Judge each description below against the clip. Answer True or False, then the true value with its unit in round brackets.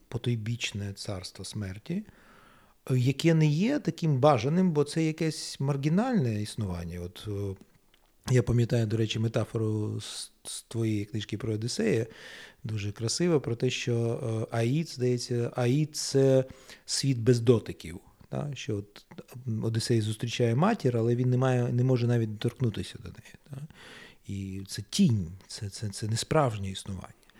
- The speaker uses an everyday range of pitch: True (4.3 semitones)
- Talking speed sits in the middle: True (140 wpm)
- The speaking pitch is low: True (120 Hz)